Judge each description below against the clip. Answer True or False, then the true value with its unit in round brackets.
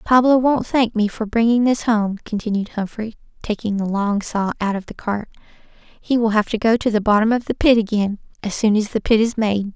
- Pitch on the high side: True (220 Hz)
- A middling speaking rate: False (230 wpm)